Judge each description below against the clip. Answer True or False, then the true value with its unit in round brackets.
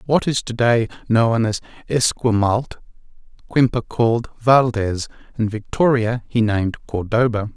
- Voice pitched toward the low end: True (115 Hz)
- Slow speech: True (120 wpm)